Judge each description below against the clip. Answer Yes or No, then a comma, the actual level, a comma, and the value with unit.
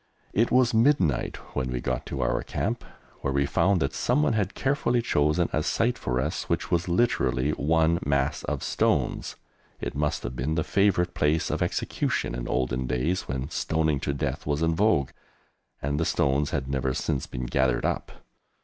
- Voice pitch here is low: Yes, very low, 75 Hz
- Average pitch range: Yes, average, 4.9 semitones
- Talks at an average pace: Yes, average, 180 wpm